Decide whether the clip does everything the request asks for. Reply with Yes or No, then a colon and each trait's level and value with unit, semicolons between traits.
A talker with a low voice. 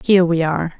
No: medium, 170 Hz